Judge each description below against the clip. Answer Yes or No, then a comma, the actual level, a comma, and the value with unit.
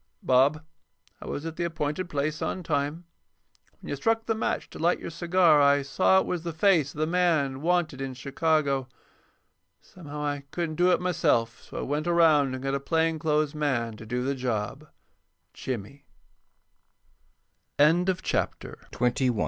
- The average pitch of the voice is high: No, medium, 150 Hz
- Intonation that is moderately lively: Yes, average, 3.5 semitones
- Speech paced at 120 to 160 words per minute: Yes, average, 155 wpm